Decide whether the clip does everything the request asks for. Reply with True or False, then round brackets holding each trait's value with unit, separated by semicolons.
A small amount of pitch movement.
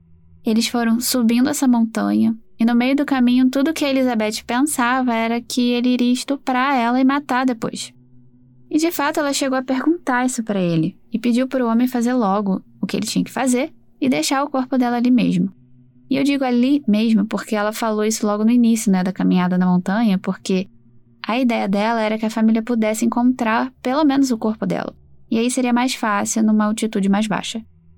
False (3.7 semitones)